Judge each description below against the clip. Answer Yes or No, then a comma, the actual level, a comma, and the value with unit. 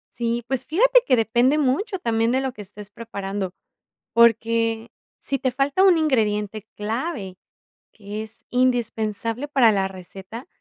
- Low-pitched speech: No, high, 230 Hz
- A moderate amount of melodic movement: Yes, average, 3.9 semitones